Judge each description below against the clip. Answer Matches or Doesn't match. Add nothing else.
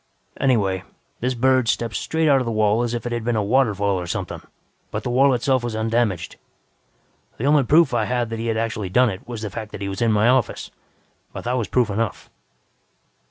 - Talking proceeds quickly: Matches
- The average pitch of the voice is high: Doesn't match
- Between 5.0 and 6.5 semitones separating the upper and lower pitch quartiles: Doesn't match